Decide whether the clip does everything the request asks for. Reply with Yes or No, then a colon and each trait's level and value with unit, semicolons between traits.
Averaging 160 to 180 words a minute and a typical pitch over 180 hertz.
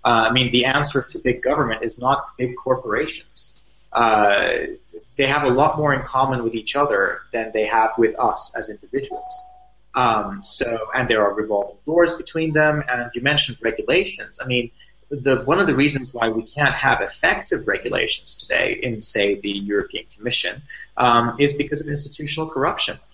No: average, 175 wpm; low, 130 Hz